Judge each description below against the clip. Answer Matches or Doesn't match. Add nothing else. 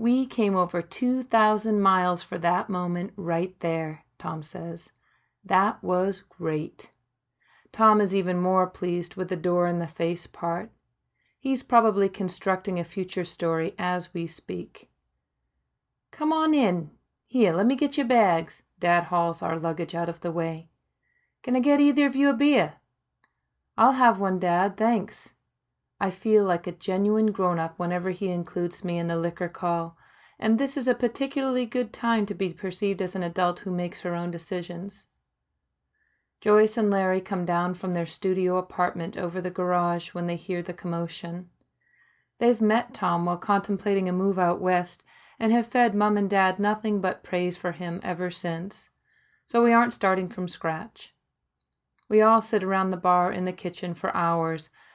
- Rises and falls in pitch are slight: Doesn't match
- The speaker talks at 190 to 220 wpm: Doesn't match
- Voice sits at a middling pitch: Matches